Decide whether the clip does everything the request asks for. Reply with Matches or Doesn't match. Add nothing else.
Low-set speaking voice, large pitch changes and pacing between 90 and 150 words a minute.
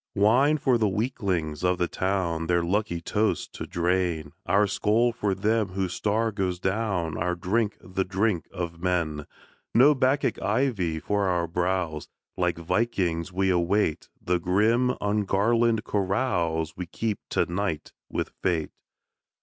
Doesn't match